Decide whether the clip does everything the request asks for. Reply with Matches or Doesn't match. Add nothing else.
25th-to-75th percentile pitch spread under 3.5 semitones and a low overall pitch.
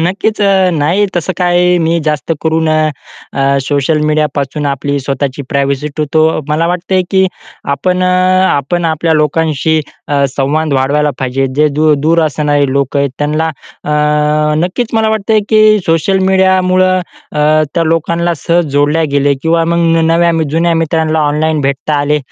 Doesn't match